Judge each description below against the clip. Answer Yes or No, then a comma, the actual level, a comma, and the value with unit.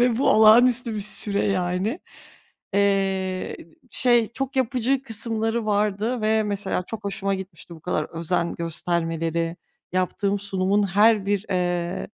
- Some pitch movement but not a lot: Yes, average, 3.5 semitones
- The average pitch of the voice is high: Yes, high, 200 Hz